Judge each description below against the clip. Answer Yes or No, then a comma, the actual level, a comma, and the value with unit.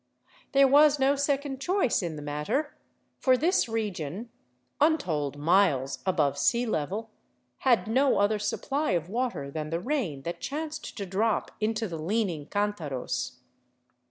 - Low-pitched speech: No, high, 210 Hz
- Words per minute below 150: Yes, average, 140 wpm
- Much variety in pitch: Yes, wide, 8.7 semitones